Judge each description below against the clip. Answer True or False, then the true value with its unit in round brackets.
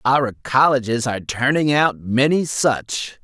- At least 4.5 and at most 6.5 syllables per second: False (4.1 syllables/s)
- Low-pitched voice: True (130 Hz)